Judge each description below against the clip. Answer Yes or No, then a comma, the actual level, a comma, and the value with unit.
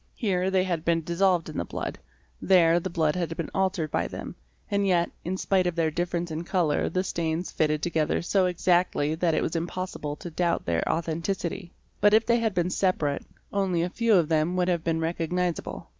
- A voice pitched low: No, medium, 175 Hz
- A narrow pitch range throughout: Yes, narrow, 2.2 semitones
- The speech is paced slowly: No, fast, 205 wpm